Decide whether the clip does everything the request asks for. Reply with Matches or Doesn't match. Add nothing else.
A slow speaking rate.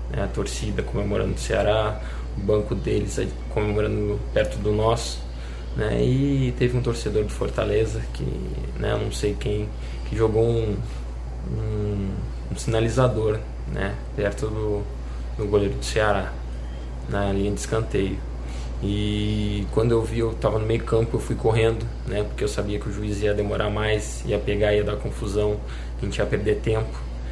Doesn't match